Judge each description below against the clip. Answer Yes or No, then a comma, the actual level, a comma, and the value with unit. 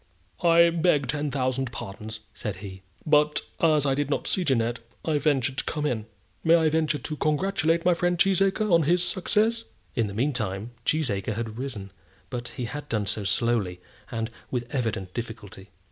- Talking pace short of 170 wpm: No, average, 175 wpm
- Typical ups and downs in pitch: No, wide, 6.2 semitones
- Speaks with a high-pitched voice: No, low, 135 Hz